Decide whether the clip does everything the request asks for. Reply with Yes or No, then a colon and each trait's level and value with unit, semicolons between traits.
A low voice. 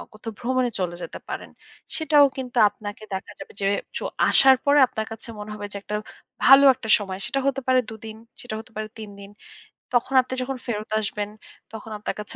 No: high, 225 Hz